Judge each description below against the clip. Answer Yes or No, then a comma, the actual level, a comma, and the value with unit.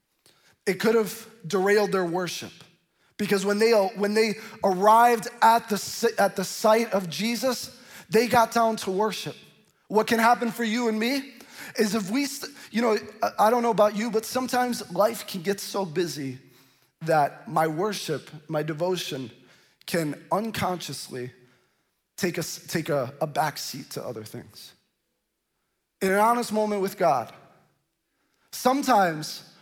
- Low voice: No, high, 205 Hz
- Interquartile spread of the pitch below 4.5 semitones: No, average, 4.8 semitones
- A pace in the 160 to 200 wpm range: No, average, 145 wpm